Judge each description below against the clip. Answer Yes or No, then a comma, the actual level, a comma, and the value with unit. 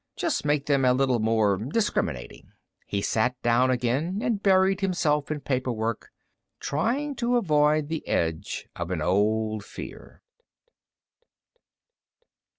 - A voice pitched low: Yes, low, 130 Hz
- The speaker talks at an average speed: No, slow, 120 wpm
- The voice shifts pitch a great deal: Yes, wide, 6.7 semitones